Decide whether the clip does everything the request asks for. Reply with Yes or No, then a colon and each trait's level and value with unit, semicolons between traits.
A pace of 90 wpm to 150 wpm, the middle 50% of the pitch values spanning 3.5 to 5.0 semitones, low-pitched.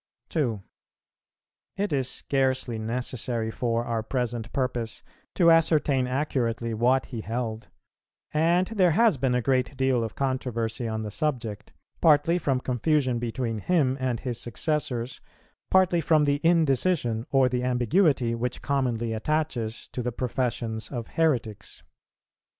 Yes: slow, 135 wpm; average, 4.0 semitones; low, 125 Hz